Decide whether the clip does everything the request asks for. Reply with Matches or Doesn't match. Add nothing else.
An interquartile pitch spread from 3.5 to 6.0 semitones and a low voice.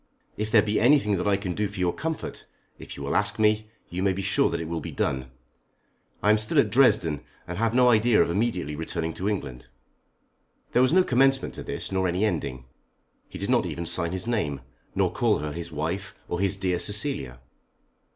Matches